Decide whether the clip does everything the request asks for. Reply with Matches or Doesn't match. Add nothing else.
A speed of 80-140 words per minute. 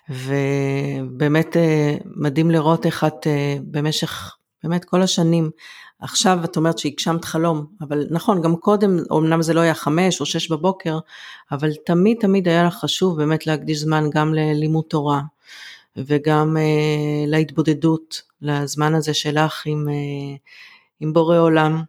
Matches